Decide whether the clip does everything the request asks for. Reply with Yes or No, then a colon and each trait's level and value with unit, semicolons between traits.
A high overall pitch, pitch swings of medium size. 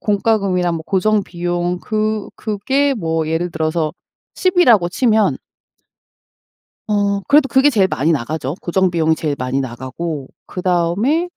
No: medium, 180 Hz; average, 5.0 semitones